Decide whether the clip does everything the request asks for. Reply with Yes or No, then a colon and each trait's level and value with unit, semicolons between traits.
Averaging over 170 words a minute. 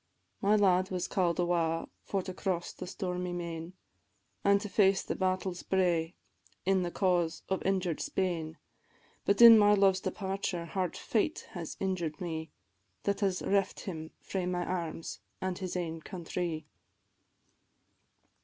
No: average, 145 wpm